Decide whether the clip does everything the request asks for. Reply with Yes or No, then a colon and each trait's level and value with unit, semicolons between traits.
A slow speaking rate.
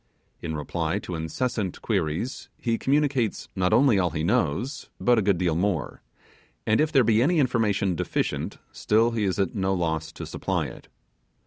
No: average, 175 wpm